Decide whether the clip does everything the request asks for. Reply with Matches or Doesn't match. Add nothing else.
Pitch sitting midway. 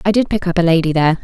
Matches